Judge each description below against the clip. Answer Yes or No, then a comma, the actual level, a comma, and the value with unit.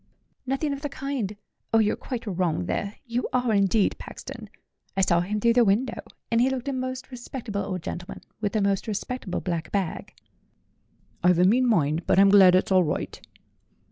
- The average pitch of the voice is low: No, high, 210 Hz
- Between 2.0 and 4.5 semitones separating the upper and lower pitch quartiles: No, average, 5.1 semitones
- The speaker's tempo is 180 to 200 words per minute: Yes, average, 185 wpm